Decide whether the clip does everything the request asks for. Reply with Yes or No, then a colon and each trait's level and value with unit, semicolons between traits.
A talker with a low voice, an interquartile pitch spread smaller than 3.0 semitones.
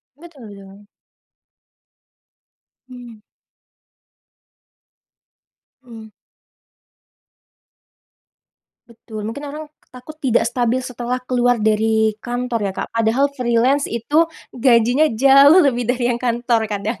No: high, 240 Hz; narrow, 2.6 semitones